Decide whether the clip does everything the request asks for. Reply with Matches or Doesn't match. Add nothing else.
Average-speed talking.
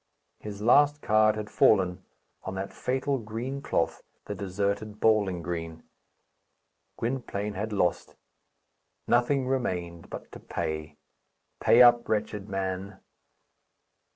Doesn't match